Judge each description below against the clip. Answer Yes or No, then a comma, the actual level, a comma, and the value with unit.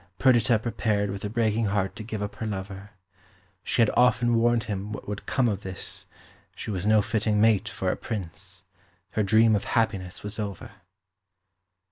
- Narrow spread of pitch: Yes, narrow, 2.2 semitones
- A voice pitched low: Yes, low, 105 Hz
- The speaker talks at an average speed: Yes, average, 175 wpm